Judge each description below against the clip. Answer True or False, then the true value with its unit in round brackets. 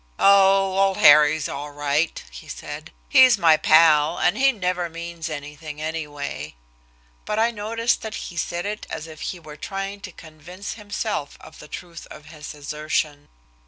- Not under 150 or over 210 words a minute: True (160 wpm)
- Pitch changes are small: False (4.4 semitones)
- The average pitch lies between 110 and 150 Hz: False (165 Hz)